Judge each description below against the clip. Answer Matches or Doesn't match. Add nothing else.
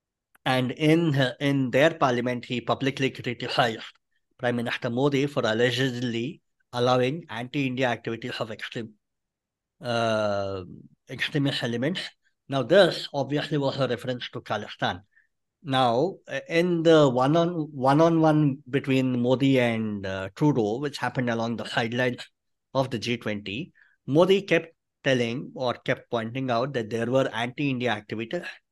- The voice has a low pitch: Matches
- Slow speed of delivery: Matches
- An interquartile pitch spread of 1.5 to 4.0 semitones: Matches